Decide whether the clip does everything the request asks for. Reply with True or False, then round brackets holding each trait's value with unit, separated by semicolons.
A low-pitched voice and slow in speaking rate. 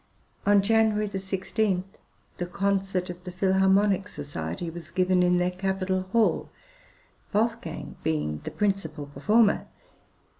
False (190 Hz; 115 wpm)